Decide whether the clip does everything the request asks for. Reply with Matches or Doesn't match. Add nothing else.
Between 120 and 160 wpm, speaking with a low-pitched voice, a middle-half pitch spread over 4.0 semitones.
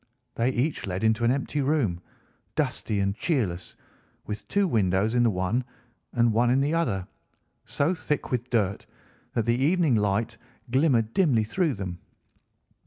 Matches